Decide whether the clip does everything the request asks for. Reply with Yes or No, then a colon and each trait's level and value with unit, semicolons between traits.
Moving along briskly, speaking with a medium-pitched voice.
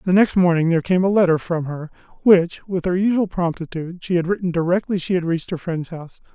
Yes: fast, 225 wpm; medium, 175 Hz